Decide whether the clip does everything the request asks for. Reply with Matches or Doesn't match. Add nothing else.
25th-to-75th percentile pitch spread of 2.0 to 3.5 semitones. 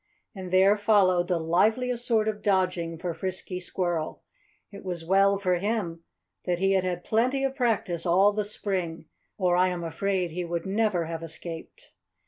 Matches